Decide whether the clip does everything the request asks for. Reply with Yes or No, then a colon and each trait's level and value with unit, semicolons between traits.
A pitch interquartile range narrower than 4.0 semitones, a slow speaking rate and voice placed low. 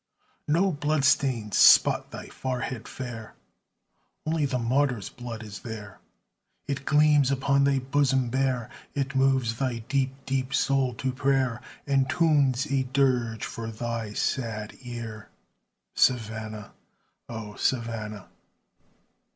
Yes: average, 3.3 semitones; slow, 120 wpm; low, 130 Hz